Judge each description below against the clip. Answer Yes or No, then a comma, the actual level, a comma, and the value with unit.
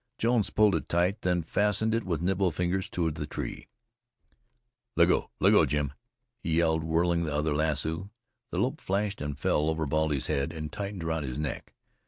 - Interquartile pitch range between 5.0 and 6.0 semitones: No, average, 3.8 semitones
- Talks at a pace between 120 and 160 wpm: No, average, 185 wpm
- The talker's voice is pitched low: Yes, very low, 80 Hz